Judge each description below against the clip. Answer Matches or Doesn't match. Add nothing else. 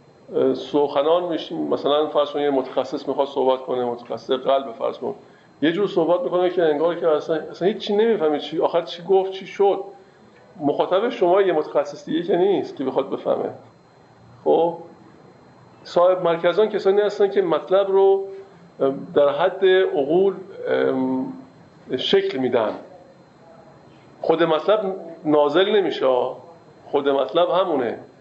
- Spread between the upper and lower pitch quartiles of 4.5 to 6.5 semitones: Matches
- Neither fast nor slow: Matches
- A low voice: Doesn't match